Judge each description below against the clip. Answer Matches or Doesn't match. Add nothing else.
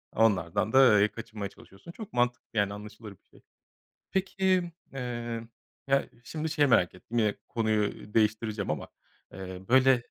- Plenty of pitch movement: Doesn't match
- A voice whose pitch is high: Doesn't match